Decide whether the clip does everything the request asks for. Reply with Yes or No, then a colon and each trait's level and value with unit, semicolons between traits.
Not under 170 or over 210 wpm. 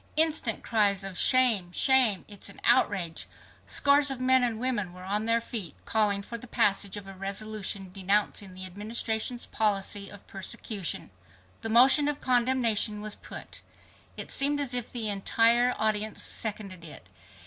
No: average, 160 wpm